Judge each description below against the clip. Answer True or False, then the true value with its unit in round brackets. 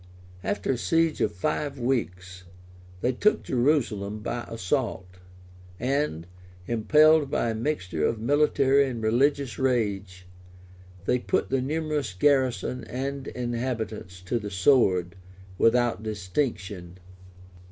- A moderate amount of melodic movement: False (5.7 semitones)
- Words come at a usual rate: False (110 wpm)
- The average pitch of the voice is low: True (120 Hz)